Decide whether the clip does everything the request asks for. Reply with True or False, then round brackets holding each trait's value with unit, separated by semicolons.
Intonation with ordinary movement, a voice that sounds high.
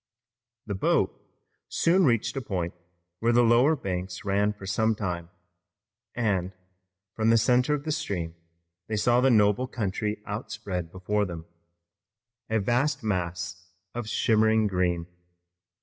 False (4.3 semitones; 105 Hz)